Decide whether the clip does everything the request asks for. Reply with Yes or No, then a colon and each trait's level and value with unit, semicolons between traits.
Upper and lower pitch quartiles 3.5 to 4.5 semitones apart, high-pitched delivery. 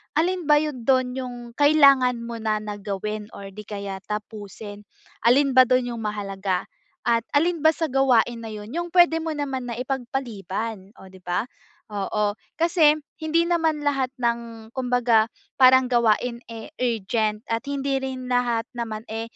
Yes: average, 4.2 semitones; high, 240 Hz